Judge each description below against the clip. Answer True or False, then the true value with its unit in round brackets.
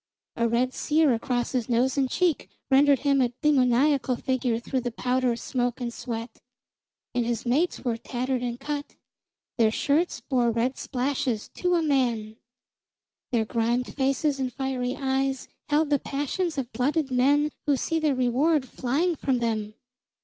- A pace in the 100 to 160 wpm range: True (155 wpm)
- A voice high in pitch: True (255 Hz)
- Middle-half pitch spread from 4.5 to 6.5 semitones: False (2.9 semitones)